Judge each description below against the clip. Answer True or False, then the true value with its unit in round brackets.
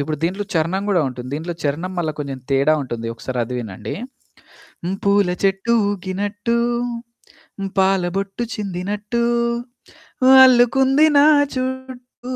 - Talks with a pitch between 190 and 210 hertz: True (195 Hz)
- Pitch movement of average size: False (7.0 semitones)